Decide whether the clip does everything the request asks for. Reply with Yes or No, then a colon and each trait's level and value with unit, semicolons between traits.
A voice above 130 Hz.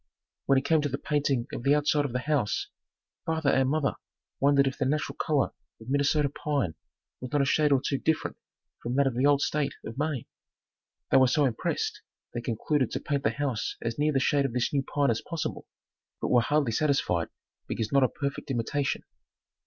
Yes: medium, 140 Hz